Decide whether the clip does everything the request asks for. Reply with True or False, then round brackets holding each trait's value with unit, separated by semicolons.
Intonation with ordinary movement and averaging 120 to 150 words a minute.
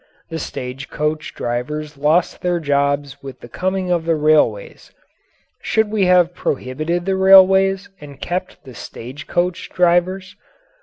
True (4.4 semitones; 140 wpm)